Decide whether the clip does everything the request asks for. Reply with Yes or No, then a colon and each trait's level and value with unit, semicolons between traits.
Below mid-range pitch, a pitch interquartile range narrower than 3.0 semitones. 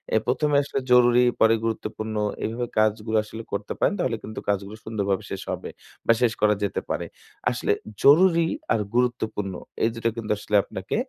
Yes: low, 110 Hz; narrow, 2.5 semitones